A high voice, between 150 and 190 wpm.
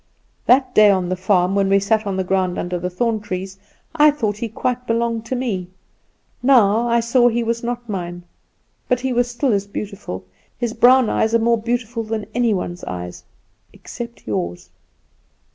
Yes: high, 220 Hz; average, 180 wpm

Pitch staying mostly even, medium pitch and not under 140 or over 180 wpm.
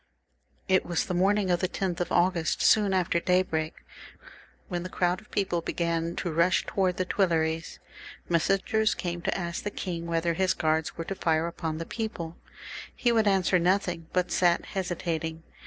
Yes: narrow, 2.1 semitones; medium, 175 Hz; average, 170 wpm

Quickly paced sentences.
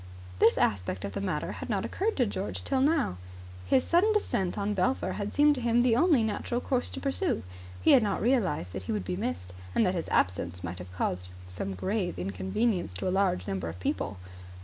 Yes: fast, 210 wpm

